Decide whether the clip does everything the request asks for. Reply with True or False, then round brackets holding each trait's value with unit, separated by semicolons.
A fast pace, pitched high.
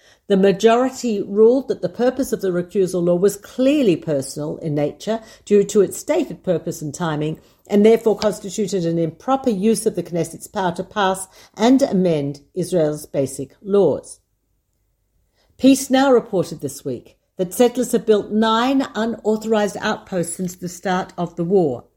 True (155 wpm; 195 Hz)